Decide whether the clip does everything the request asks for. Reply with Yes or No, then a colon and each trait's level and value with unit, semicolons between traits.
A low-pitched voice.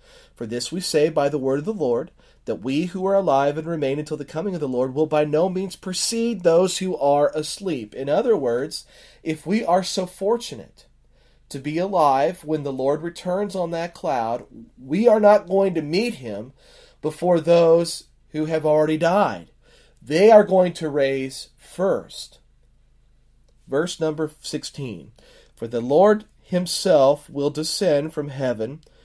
No: medium, 165 Hz